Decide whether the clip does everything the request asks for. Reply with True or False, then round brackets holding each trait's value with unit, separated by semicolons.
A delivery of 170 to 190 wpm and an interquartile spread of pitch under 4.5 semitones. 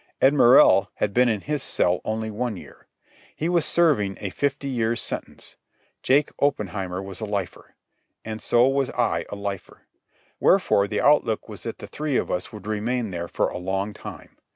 False (180 wpm; 5.1 semitones)